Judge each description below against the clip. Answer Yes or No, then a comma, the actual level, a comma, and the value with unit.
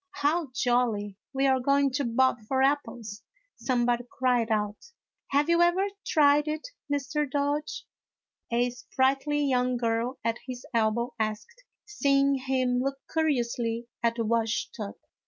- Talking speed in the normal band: Yes, average, 160 wpm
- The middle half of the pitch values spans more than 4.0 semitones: No, average, 3.3 semitones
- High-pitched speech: Yes, very high, 260 Hz